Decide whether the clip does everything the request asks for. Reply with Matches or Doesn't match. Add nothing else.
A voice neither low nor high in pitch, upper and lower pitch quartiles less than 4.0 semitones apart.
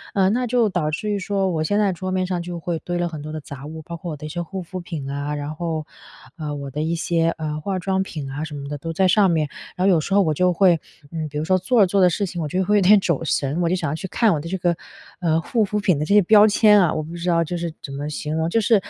Matches